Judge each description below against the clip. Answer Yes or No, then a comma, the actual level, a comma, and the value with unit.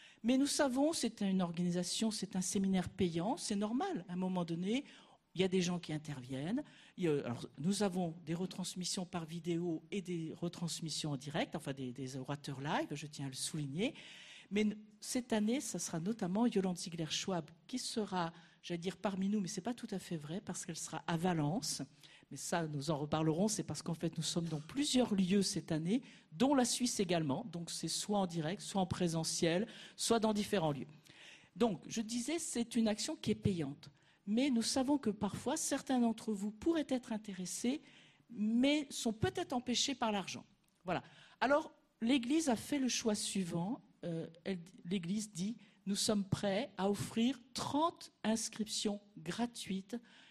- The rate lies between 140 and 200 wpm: Yes, average, 180 wpm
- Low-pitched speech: No, high, 195 Hz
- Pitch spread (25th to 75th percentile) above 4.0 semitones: Yes, wide, 5.5 semitones